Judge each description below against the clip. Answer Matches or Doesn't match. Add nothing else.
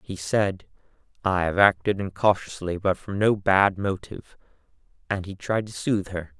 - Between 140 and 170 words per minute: Matches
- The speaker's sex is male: Matches